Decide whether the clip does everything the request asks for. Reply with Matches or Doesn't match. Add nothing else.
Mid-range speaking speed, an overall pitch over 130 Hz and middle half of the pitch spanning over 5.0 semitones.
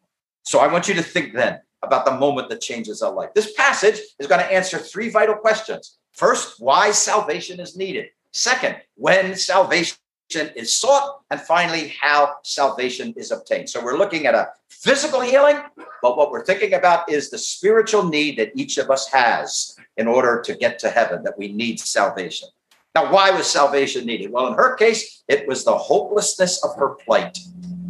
Matches